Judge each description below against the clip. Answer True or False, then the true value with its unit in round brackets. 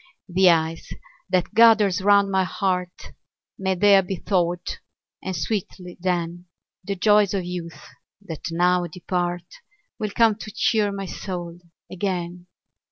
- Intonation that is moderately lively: False (2.3 semitones)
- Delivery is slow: True (130 wpm)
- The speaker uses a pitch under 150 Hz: False (185 Hz)